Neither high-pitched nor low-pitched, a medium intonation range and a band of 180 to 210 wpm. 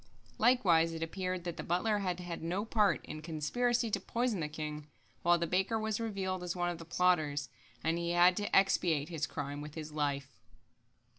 Yes: medium, 175 Hz; average, 3.8 semitones; average, 200 wpm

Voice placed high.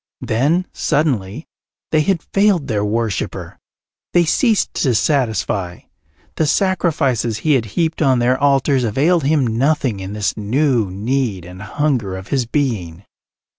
No: low, 130 Hz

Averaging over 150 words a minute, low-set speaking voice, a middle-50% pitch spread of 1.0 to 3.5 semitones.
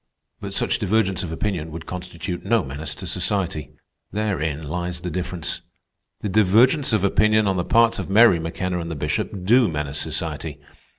No: average, 170 wpm; very low, 90 Hz; average, 4.4 semitones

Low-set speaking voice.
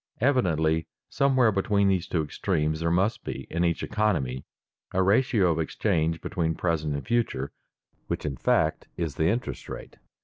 Yes: very low, 85 Hz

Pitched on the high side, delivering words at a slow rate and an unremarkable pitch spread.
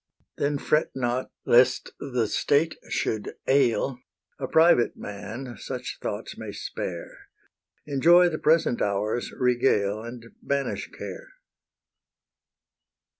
No: low, 125 Hz; slow, 105 wpm; average, 3.8 semitones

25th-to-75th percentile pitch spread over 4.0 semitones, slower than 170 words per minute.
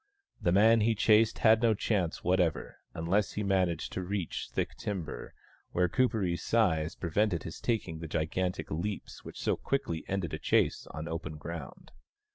Yes: average, 4.4 semitones; average, 160 wpm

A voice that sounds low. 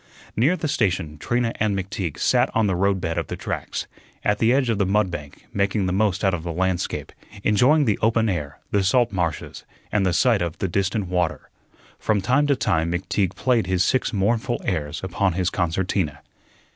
Yes: very low, 95 Hz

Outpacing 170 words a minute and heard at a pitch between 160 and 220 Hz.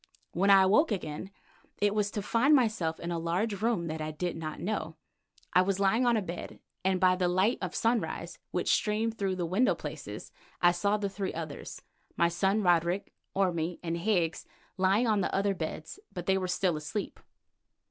Yes: average, 190 wpm; high, 190 Hz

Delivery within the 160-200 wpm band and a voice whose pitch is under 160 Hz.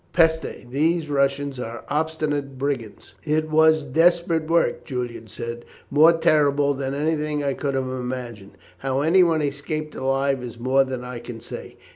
No: average, 150 wpm; medium, 140 Hz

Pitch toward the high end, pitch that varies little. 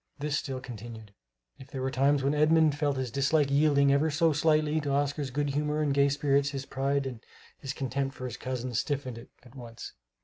No: medium, 140 Hz; narrow, 2.0 semitones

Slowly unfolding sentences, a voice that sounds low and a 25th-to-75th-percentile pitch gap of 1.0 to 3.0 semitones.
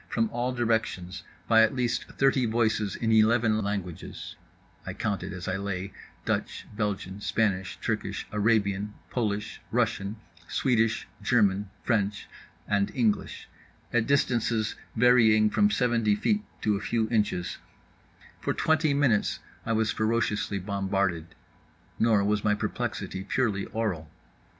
Yes: slow, 120 wpm; low, 110 Hz; average, 2.7 semitones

